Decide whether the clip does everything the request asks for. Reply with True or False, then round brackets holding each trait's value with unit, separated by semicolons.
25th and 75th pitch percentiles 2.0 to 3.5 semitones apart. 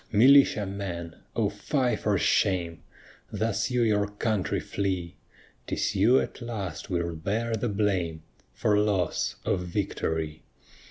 False (4.1 semitones)